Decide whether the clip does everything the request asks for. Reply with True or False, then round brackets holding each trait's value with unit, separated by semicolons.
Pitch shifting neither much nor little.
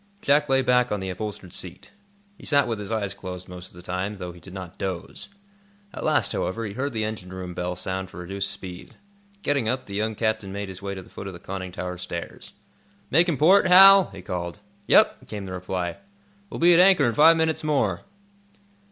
False (6.3 semitones)